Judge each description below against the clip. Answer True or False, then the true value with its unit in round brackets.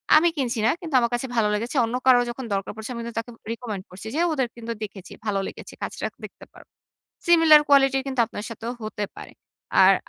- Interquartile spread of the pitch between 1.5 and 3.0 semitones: False (3.5 semitones)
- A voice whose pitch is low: False (235 Hz)